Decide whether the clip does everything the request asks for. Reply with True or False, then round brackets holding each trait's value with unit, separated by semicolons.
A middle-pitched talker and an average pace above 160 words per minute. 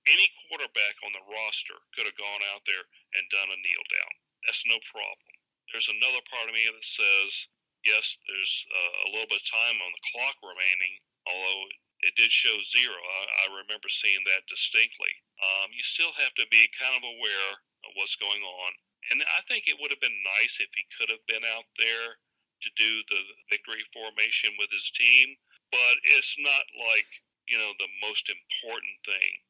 False (110 Hz; 185 wpm)